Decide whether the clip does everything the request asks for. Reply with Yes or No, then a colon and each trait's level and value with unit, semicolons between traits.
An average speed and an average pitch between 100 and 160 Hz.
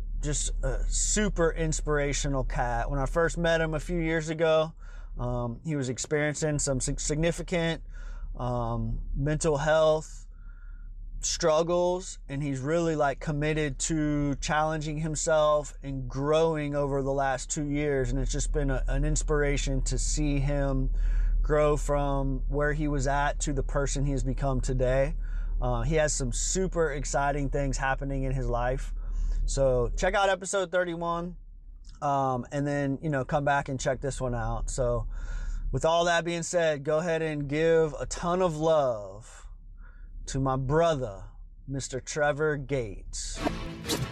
Yes: average, 150 wpm; medium, 140 Hz